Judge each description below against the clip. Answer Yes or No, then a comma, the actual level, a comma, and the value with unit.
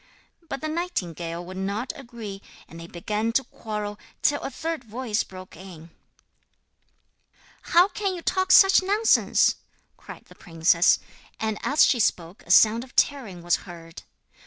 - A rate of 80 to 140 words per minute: No, average, 150 wpm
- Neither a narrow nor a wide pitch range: No, wide, 8.3 semitones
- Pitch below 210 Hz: No, high, 215 Hz